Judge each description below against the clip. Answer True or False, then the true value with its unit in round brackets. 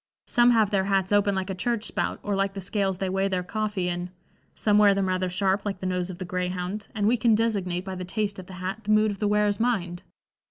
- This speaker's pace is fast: True (255 wpm)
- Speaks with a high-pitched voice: True (195 Hz)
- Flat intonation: True (2.2 semitones)